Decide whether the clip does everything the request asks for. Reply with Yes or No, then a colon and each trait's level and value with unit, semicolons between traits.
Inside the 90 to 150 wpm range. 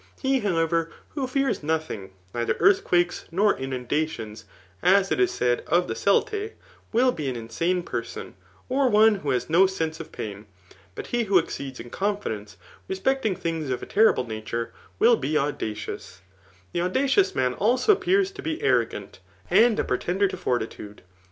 No: average, 165 wpm